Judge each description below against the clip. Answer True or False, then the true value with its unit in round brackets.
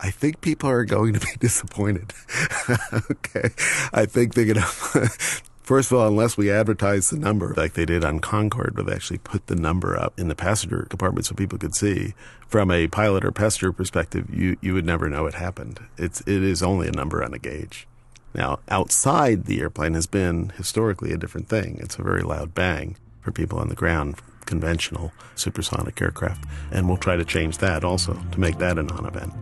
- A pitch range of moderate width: True (4.2 semitones)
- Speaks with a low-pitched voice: True (100 Hz)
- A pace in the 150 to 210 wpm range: True (200 wpm)